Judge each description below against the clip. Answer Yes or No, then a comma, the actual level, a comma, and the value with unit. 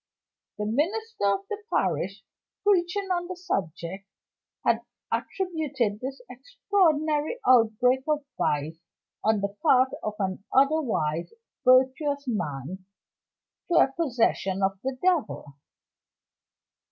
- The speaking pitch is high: Yes, very high, 255 Hz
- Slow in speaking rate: Yes, slow, 105 wpm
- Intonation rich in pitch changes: Yes, wide, 8.1 semitones